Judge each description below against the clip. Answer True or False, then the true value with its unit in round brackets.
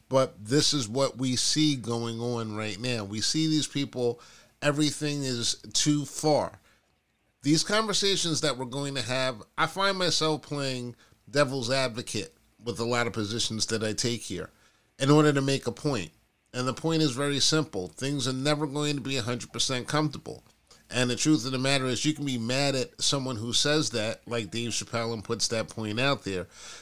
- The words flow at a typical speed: True (190 wpm)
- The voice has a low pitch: True (130 Hz)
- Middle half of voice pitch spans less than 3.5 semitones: False (4.2 semitones)